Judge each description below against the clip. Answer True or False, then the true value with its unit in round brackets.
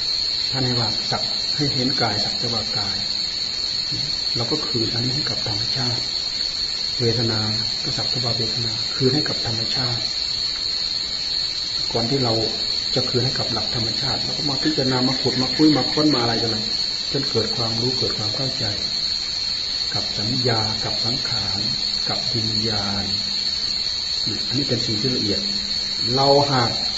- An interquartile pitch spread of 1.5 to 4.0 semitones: True (2.7 semitones)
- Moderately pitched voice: False (115 Hz)